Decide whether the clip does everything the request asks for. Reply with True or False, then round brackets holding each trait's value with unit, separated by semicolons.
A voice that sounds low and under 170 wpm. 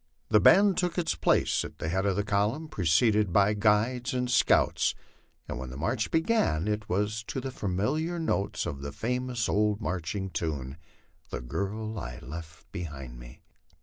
False (105 Hz; 180 wpm)